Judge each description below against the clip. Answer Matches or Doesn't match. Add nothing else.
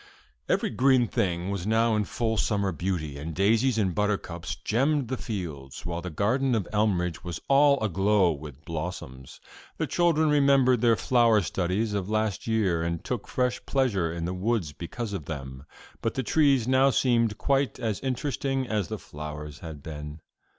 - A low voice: Matches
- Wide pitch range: Matches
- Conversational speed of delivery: Matches